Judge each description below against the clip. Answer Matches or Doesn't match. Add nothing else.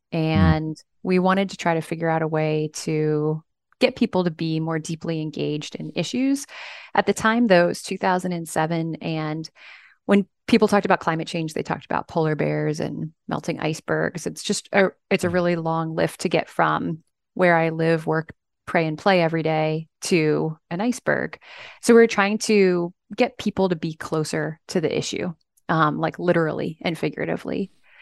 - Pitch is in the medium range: Matches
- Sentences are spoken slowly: Doesn't match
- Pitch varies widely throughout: Doesn't match